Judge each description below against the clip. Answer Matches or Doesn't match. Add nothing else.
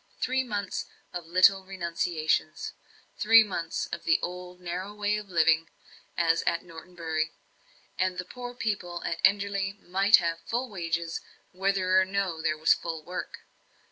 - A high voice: Doesn't match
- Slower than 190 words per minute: Matches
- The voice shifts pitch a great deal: Doesn't match